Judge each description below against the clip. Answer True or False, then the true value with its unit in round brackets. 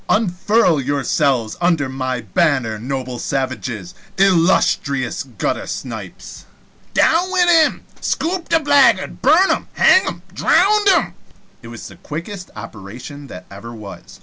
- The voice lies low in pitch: False (145 Hz)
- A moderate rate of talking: False (125 wpm)